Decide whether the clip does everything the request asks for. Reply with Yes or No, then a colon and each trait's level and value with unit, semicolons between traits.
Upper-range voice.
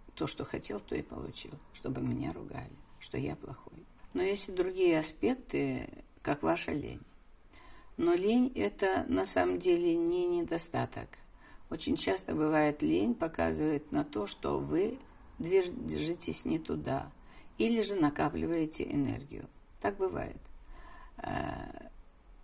Yes: high, 195 Hz